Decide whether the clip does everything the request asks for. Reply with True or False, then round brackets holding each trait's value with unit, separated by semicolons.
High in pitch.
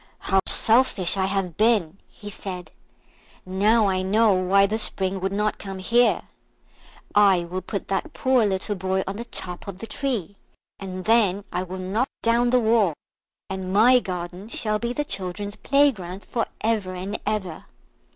True (200 Hz)